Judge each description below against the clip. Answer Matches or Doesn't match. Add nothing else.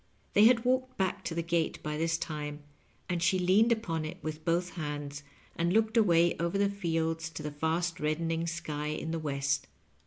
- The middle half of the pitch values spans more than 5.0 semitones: Doesn't match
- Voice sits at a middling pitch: Matches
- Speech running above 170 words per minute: Matches